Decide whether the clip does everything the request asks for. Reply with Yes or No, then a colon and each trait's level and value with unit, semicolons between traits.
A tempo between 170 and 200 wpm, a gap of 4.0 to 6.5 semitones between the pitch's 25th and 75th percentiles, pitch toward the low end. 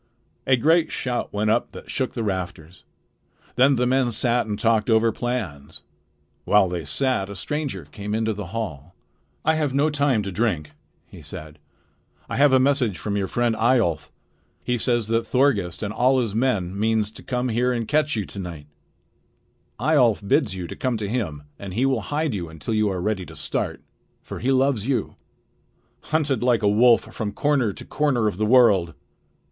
Yes: average, 185 wpm; average, 4.5 semitones; low, 115 Hz